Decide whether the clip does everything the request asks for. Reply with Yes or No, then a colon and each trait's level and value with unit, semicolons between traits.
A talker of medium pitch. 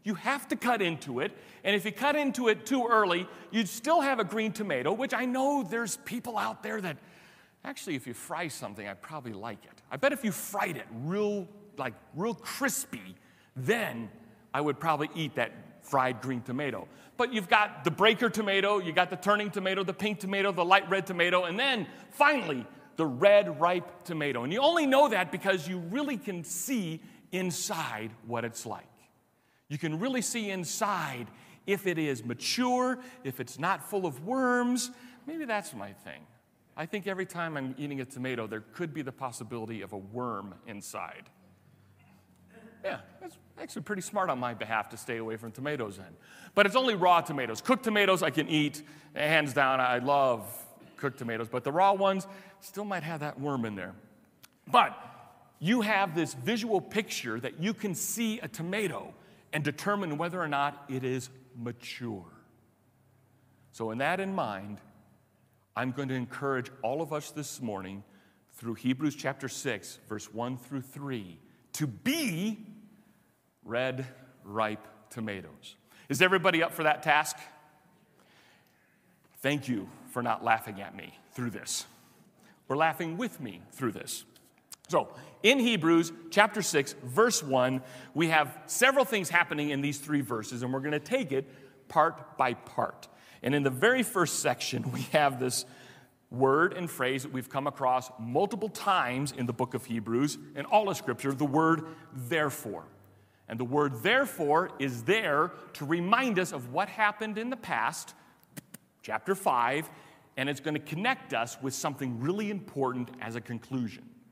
Yes: medium, 155 Hz